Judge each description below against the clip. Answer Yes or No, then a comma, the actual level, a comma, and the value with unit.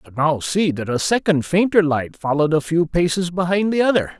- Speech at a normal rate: No, fast, 230 wpm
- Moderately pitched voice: Yes, medium, 165 Hz